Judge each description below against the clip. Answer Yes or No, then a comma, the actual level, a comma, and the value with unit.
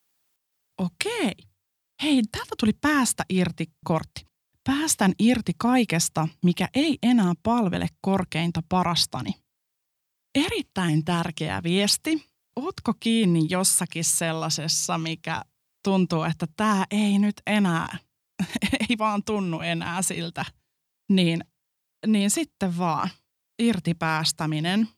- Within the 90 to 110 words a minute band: Yes, slow, 95 wpm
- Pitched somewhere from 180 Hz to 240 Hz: Yes, medium, 185 Hz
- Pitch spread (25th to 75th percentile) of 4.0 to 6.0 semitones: Yes, average, 5.1 semitones